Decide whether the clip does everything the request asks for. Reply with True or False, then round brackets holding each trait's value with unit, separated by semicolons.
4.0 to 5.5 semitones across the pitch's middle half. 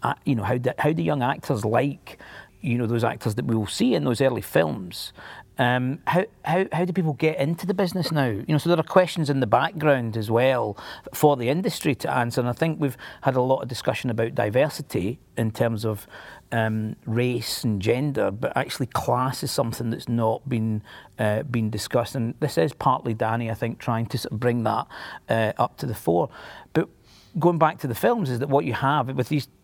True (4.5 semitones)